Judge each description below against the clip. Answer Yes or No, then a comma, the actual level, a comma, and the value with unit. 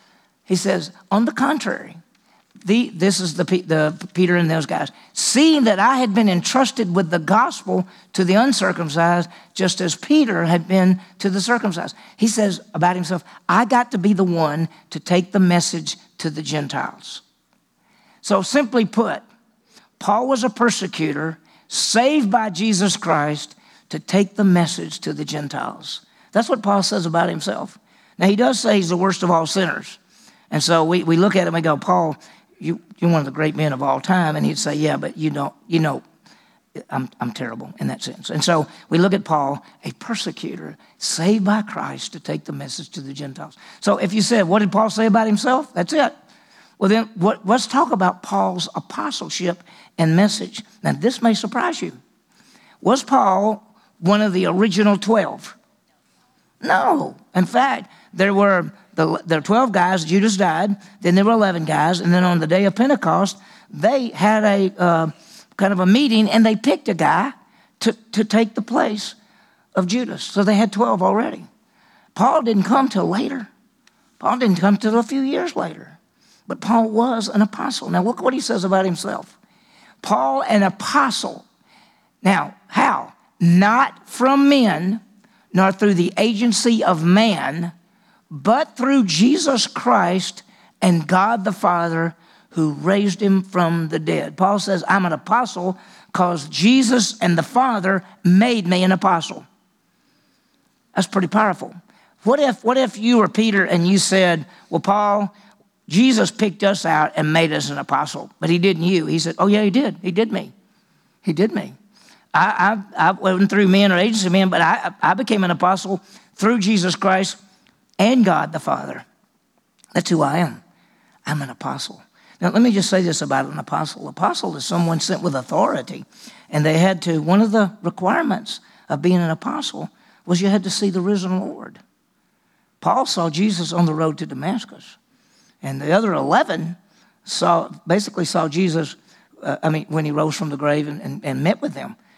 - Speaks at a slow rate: No, average, 180 wpm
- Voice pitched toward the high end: Yes, high, 195 Hz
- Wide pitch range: No, average, 4.1 semitones